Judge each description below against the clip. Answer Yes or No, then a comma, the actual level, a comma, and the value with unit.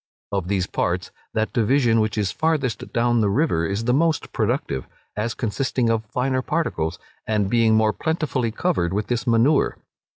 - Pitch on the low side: Yes, low, 115 Hz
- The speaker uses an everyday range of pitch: Yes, average, 4.0 semitones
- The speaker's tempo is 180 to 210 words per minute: No, average, 165 wpm